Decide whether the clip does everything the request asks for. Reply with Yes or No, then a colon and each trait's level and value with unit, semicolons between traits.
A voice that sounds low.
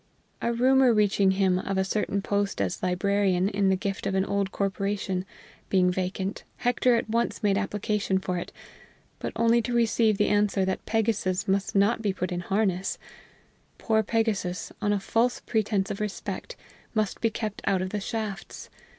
No: high, 200 Hz